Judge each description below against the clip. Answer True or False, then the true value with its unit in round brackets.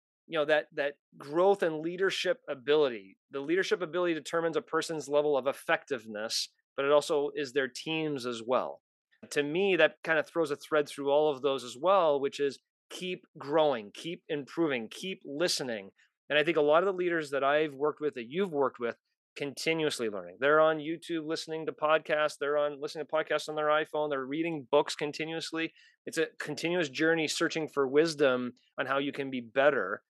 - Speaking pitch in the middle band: True (150 Hz)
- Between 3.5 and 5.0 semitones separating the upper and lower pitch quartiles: False (2.4 semitones)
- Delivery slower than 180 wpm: False (190 wpm)